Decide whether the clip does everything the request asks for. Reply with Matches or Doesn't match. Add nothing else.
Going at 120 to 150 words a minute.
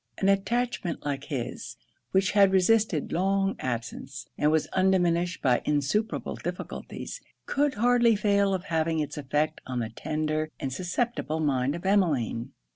Matches